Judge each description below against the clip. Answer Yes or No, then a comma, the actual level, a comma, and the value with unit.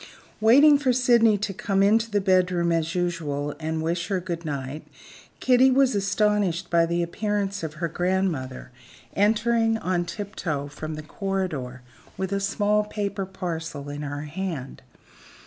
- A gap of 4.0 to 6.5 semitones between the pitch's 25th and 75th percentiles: Yes, average, 4.5 semitones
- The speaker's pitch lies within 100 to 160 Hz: No, medium, 185 Hz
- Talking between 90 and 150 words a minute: Yes, average, 145 wpm